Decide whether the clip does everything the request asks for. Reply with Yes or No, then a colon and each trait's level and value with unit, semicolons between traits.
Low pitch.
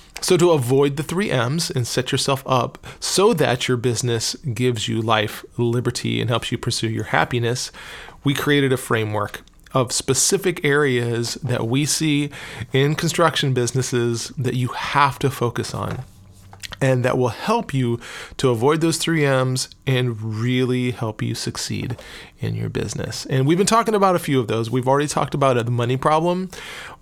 Yes: low, 130 Hz